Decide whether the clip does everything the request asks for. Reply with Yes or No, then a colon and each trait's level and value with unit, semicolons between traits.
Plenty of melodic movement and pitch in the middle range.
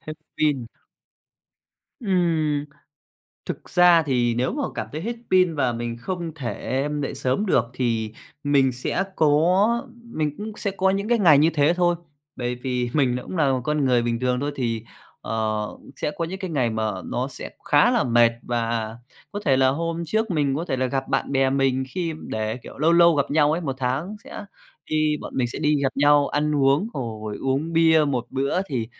No: average, 4.8 semitones; medium, 145 Hz